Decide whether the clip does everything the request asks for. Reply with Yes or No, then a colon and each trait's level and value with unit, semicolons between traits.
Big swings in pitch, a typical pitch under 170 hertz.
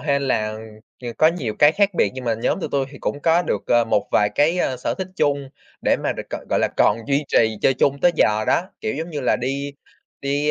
No: average, 4.3 semitones; medium, 140 Hz